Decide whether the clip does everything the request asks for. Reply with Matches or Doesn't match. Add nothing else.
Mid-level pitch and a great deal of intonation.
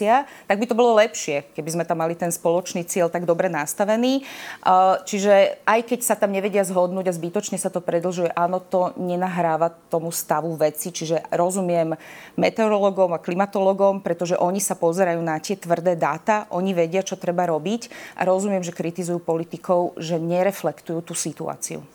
Doesn't match